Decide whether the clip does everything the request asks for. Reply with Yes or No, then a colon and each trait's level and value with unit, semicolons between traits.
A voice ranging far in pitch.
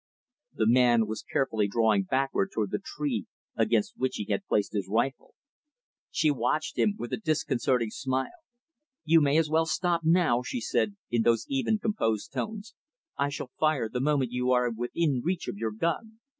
Yes: wide, 6.1 semitones